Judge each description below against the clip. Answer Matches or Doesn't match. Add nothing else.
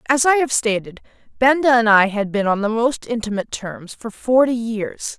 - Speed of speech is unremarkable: Matches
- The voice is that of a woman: Matches